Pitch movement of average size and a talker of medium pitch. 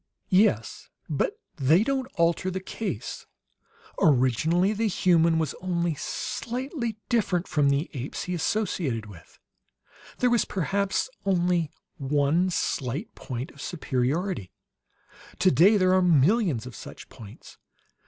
No: wide, 5.7 semitones; medium, 175 Hz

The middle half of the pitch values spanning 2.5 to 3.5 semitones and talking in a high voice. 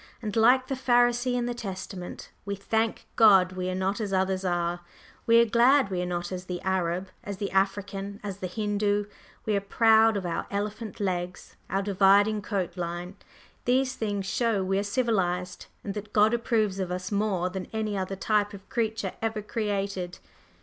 Yes: average, 2.8 semitones; high, 200 Hz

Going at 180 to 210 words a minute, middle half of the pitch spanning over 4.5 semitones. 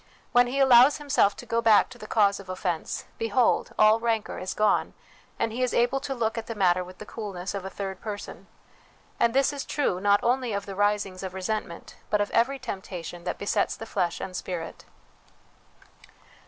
No: average, 195 wpm; average, 3.8 semitones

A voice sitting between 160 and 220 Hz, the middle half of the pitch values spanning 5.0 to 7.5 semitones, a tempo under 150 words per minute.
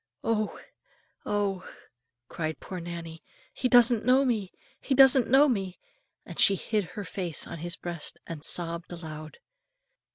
Yes: high, 190 Hz; wide, 5.6 semitones; average, 140 wpm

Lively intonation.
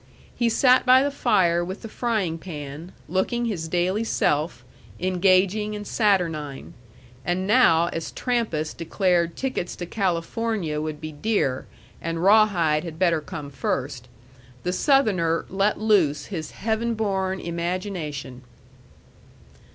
No: average, 4.8 semitones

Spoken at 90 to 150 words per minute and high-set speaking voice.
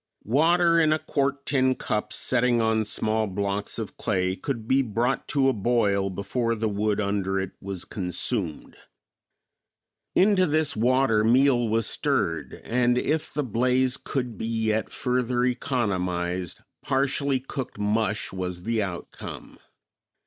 No: slow, 135 wpm; low, 115 Hz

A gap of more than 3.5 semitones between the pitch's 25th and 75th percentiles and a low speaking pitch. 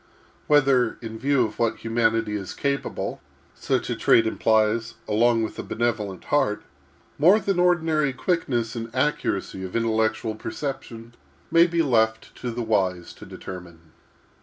Yes: average, 3.9 semitones; low, 115 Hz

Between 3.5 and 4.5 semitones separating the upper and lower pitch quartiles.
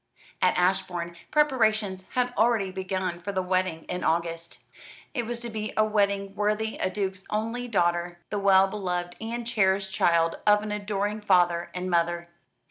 No: average, 3.1 semitones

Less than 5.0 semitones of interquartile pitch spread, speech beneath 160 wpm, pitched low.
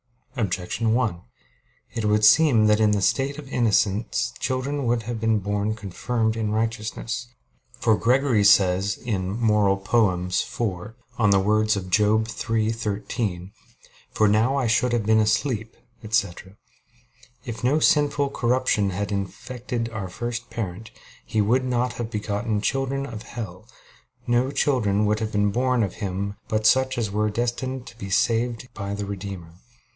Yes: average, 2.9 semitones; average, 150 wpm; low, 110 Hz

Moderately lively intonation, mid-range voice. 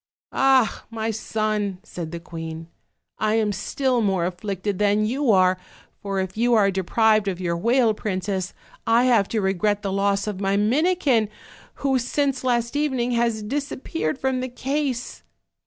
No: average, 4.2 semitones; high, 215 Hz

